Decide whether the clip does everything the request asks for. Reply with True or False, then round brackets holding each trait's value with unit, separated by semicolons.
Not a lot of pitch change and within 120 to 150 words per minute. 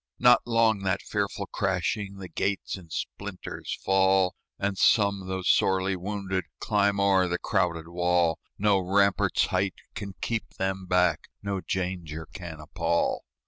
True (2.0 semitones; 140 wpm)